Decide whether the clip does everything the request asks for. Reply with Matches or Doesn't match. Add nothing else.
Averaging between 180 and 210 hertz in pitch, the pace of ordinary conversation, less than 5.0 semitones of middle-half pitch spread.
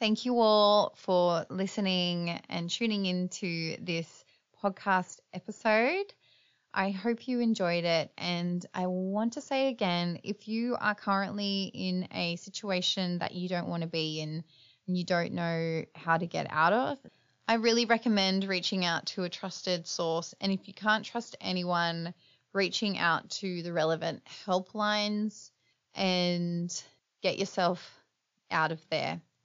Matches